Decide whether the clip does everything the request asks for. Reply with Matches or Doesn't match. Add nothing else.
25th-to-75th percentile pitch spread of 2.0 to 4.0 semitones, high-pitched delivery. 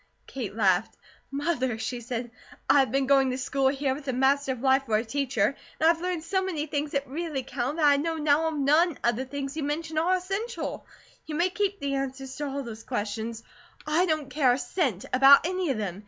Matches